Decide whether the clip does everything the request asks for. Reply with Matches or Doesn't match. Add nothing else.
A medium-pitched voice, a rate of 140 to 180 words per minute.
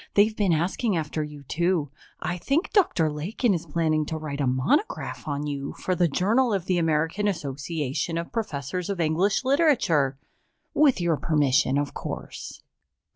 Matches